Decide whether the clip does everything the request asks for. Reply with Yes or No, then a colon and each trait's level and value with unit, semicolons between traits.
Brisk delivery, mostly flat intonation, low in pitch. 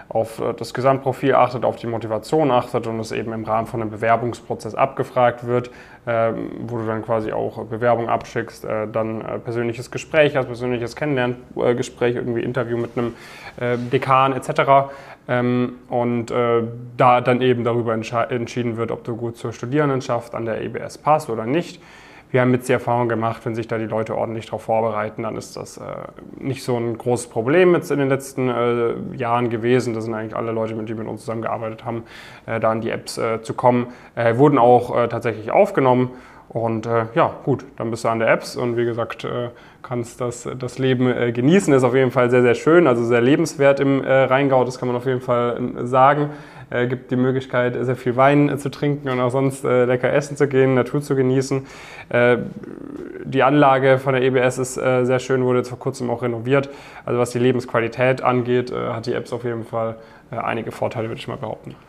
Yes: fast, 200 wpm; narrow, 2.1 semitones; low, 125 Hz